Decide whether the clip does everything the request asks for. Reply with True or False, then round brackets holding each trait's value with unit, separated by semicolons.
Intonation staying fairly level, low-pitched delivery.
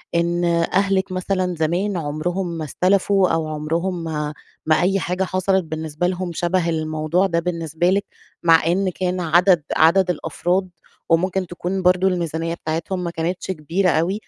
False (2.3 semitones; 175 Hz)